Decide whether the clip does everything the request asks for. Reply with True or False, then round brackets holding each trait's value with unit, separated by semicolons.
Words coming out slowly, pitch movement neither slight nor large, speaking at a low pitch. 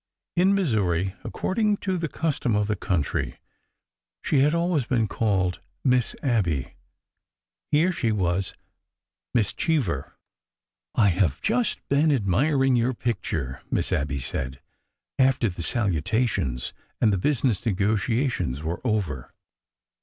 False (125 wpm; 7.5 semitones; 110 Hz)